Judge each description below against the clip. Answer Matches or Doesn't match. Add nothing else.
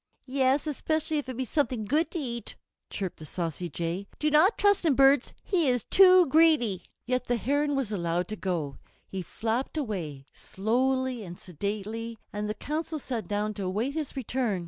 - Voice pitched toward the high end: Matches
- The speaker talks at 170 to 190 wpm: Matches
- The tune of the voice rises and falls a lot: Matches